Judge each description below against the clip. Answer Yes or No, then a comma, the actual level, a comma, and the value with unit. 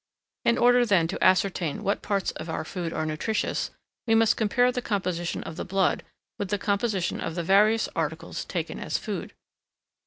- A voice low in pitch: No, high, 195 Hz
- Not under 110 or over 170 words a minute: No, average, 180 wpm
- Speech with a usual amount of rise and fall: Yes, average, 4.2 semitones